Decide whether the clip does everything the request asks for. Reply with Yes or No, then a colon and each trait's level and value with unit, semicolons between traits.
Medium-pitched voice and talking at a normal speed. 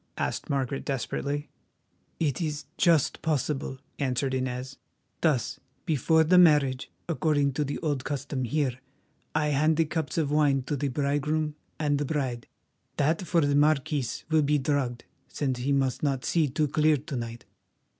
Yes: medium, 145 Hz; average, 155 wpm